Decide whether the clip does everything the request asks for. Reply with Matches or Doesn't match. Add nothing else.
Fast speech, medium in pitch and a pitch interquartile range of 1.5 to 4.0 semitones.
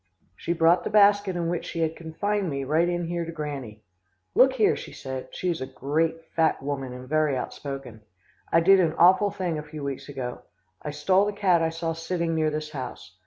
Matches